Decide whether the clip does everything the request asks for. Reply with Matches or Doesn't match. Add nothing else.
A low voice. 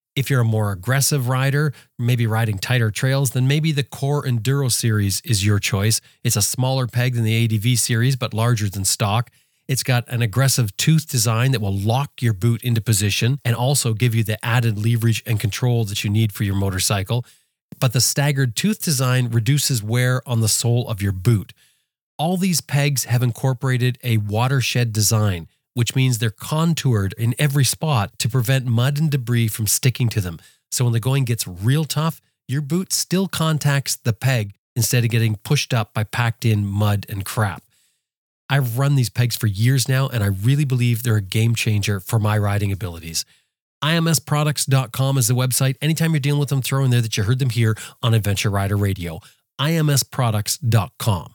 Matches